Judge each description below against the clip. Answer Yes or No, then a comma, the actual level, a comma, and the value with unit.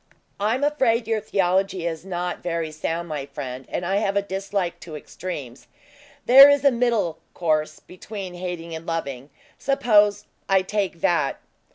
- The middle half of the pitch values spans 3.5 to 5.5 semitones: Yes, average, 4.1 semitones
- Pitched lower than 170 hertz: No, medium, 180 Hz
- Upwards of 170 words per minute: No, average, 160 wpm